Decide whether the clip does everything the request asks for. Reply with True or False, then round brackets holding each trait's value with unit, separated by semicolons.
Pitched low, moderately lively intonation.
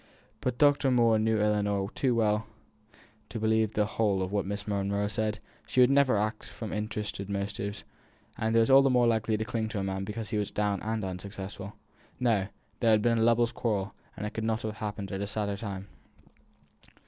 False (105 Hz; 1.9 semitones)